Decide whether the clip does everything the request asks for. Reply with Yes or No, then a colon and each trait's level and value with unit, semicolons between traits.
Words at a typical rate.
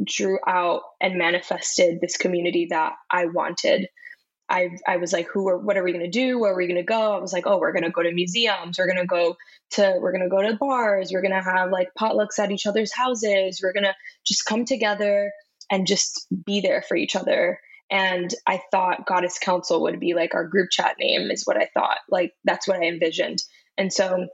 No: fast, 215 wpm